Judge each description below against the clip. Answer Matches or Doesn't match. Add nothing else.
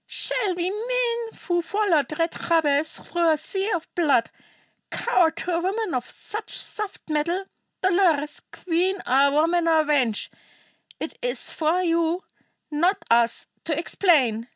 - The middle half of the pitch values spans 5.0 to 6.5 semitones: Doesn't match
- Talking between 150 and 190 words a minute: Doesn't match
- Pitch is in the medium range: Doesn't match